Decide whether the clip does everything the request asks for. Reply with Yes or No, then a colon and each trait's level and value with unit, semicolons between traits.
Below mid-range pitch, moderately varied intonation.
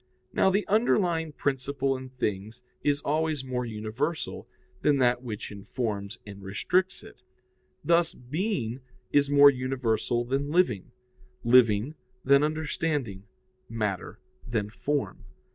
Yes: low, 130 Hz; average, 4.8 semitones